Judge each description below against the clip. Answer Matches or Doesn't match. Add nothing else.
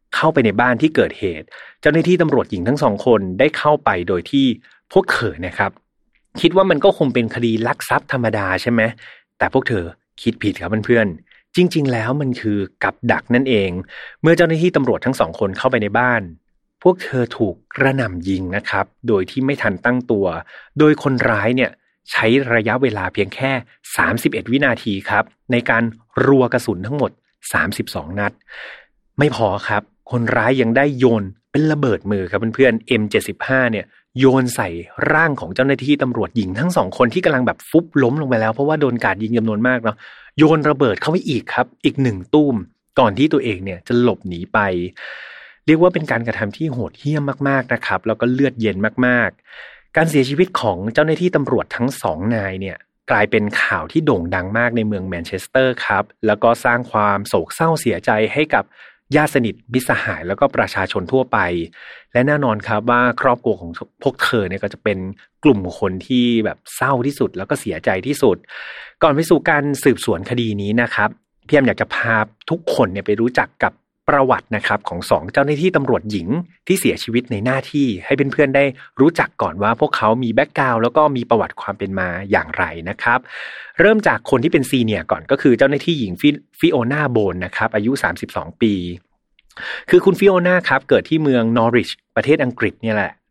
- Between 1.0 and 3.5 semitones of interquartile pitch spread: Doesn't match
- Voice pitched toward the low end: Matches